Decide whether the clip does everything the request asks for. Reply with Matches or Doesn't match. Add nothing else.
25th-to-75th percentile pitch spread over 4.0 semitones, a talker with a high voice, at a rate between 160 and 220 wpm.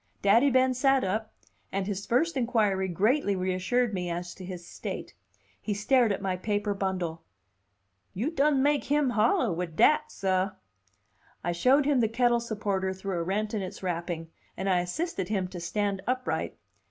Matches